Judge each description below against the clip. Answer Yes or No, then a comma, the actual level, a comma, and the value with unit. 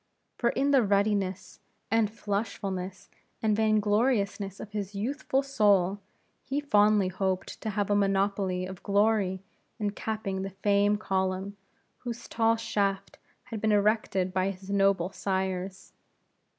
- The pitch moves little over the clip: Yes, narrow, 2.1 semitones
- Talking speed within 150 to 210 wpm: No, slow, 135 wpm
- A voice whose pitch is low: No, high, 200 Hz